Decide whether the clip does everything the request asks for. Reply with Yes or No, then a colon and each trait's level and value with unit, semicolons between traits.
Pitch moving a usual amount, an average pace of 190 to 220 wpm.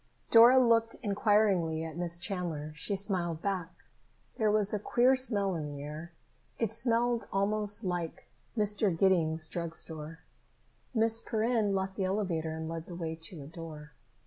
No: average, 4.7 semitones; average, 155 wpm